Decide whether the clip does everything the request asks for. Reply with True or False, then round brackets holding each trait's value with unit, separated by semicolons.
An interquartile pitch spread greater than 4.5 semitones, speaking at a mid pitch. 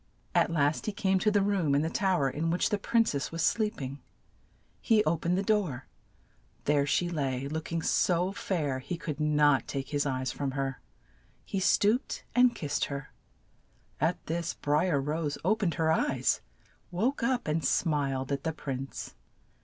True (5.1 semitones; 160 Hz)